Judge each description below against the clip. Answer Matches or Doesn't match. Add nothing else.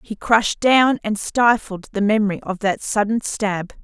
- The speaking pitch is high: Matches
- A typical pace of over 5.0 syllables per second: Doesn't match